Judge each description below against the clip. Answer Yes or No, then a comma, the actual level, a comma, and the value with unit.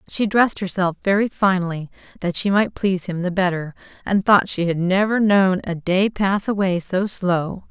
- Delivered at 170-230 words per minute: Yes, average, 185 wpm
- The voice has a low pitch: No, high, 190 Hz